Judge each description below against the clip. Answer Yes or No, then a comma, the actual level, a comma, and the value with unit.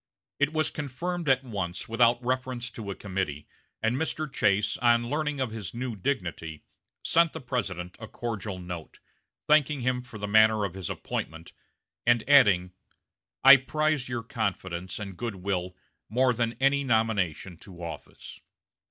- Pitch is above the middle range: No, low, 115 Hz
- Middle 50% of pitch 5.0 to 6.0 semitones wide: Yes, wide, 5.5 semitones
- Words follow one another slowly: No, average, 150 wpm